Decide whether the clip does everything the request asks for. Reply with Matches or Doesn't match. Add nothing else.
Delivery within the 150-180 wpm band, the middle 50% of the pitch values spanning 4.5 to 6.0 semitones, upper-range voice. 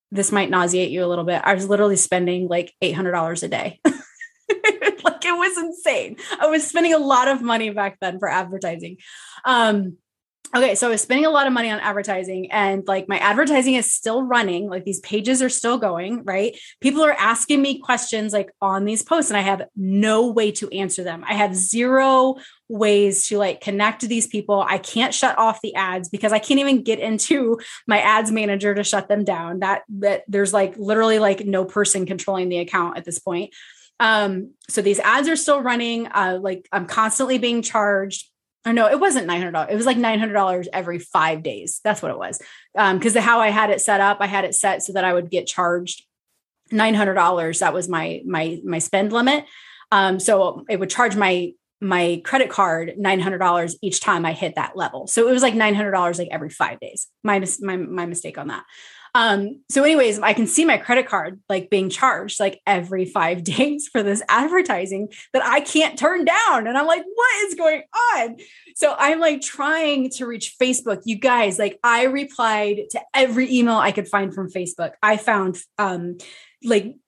Doesn't match